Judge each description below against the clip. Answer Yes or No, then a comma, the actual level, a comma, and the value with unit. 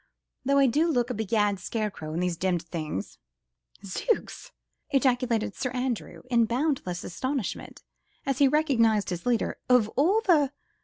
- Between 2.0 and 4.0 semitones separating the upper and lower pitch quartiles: No, wide, 5.6 semitones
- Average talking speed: Yes, average, 145 wpm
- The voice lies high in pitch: Yes, high, 240 Hz